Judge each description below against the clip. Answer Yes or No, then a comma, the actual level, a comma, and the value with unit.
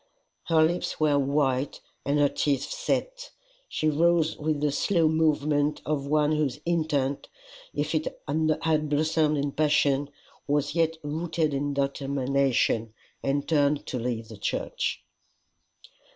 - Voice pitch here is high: No, medium, 150 Hz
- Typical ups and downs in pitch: No, narrow, 2.1 semitones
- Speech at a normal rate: No, slow, 130 wpm